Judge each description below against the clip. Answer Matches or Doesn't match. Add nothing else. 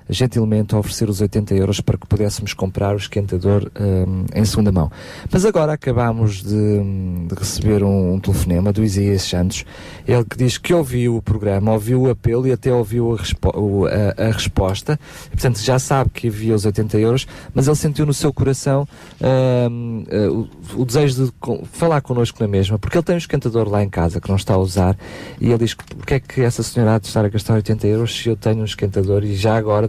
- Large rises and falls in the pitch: Doesn't match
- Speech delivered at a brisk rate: Matches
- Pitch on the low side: Matches